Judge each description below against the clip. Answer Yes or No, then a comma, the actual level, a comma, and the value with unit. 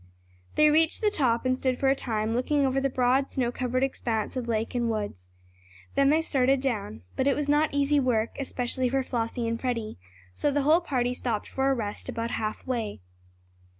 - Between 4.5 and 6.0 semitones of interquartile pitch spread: No, average, 3.0 semitones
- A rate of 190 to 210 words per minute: Yes, average, 200 wpm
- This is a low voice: No, very high, 255 Hz